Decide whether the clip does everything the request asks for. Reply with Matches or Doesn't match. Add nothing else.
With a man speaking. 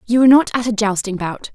Doesn't match